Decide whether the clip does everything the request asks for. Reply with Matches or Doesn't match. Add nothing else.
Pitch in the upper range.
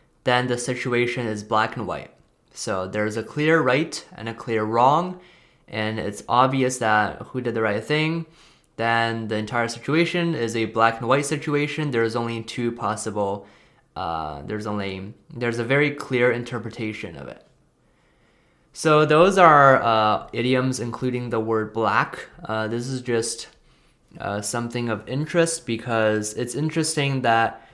Doesn't match